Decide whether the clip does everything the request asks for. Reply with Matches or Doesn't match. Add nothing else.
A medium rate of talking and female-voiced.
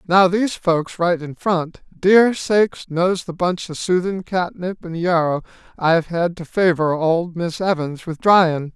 Doesn't match